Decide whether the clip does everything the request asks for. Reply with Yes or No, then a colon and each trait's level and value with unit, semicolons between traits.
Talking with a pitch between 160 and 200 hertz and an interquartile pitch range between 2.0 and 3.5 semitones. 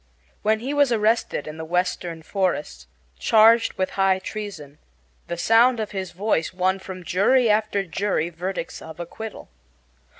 No: high, 190 Hz; average, 4.0 semitones